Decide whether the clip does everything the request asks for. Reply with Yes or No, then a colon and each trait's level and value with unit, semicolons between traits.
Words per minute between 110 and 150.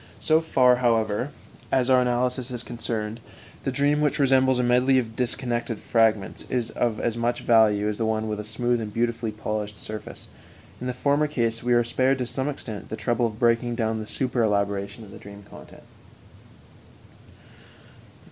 No: average, 175 wpm